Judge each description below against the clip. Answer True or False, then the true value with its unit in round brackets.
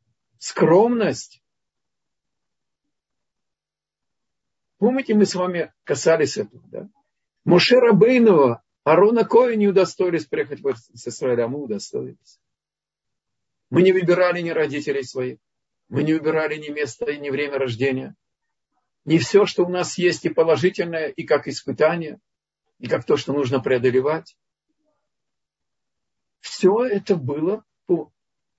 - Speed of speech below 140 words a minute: True (115 wpm)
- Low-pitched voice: False (165 Hz)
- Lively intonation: True (6.0 semitones)